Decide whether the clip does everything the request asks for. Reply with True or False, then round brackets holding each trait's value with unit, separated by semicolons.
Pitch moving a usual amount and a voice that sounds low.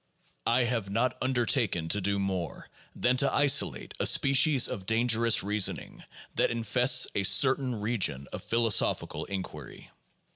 True (4.2 semitones; 115 Hz)